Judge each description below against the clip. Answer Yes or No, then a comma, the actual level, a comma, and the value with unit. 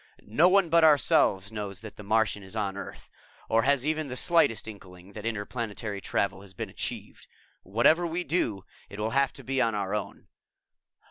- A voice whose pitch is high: No, low, 110 Hz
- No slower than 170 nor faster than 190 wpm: Yes, average, 185 wpm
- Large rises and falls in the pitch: Yes, wide, 5.7 semitones